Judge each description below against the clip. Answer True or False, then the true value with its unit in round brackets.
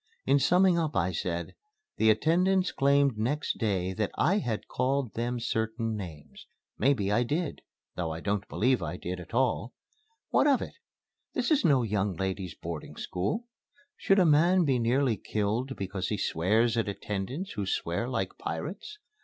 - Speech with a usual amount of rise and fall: False (6.6 semitones)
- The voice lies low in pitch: True (115 Hz)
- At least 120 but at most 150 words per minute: False (165 wpm)